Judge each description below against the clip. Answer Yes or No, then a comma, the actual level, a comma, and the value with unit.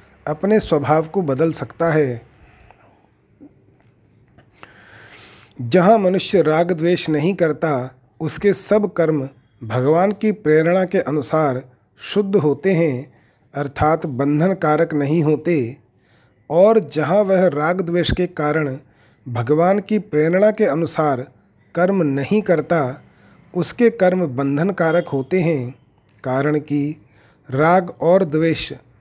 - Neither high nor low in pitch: Yes, medium, 155 Hz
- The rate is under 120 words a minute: Yes, slow, 110 wpm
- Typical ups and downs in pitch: Yes, average, 4.9 semitones